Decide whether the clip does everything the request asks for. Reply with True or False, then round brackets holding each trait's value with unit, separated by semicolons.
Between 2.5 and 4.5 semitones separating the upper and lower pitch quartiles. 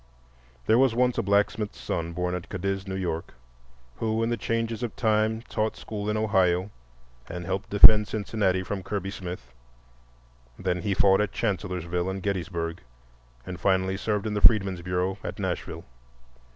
True (3.0 semitones)